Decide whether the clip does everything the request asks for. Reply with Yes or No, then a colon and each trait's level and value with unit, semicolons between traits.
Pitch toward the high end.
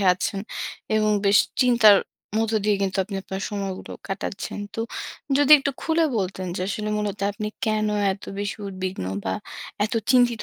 Yes: high, 210 Hz